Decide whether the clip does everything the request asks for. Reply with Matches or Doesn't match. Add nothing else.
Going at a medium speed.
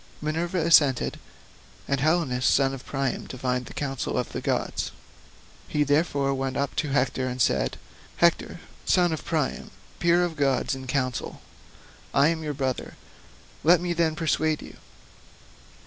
Matches